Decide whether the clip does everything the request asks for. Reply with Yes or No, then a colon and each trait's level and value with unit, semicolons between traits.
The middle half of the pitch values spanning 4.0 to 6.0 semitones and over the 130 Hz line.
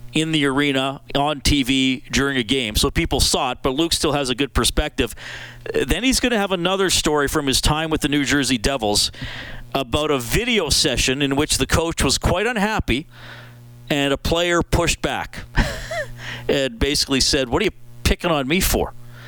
No: average, 3.3 semitones; medium, 140 Hz